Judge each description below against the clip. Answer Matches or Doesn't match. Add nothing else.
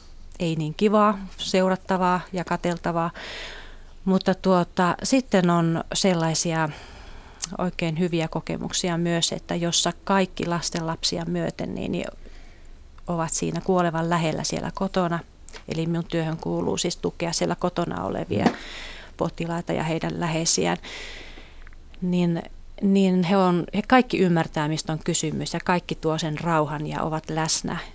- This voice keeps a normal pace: Matches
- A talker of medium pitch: Matches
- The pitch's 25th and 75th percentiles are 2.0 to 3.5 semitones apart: Matches